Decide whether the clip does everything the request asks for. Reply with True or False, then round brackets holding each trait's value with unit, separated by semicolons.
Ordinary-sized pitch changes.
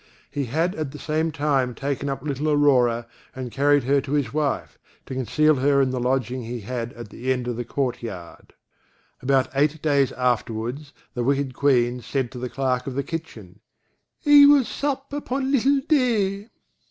True (3.6 semitones)